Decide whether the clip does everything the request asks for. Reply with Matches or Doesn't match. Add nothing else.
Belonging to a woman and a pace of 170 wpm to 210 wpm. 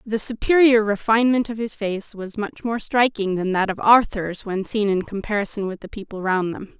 Matches